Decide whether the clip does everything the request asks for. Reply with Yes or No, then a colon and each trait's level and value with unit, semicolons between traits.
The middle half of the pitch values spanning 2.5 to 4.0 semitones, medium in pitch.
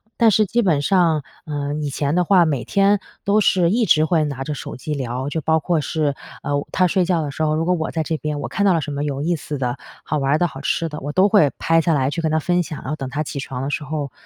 Yes: average, 3.4 semitones; medium, 155 Hz